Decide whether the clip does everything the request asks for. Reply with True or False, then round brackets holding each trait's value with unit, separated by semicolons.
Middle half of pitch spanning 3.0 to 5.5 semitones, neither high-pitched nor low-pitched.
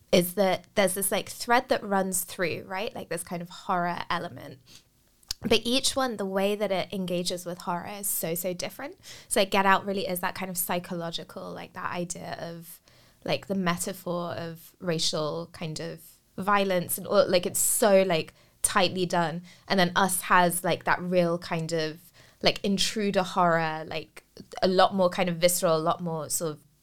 False (2.5 semitones; 180 Hz)